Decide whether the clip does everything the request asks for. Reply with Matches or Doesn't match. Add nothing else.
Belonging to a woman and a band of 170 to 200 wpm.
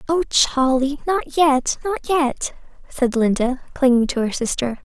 Doesn't match